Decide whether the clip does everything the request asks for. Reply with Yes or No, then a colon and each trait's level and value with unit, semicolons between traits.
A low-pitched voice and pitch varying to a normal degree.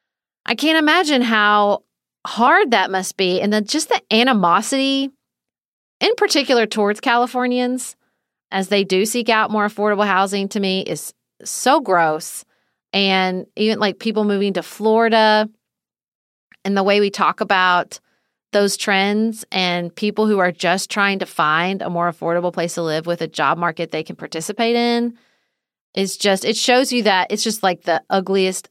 No: high, 205 Hz; average, 3.6 semitones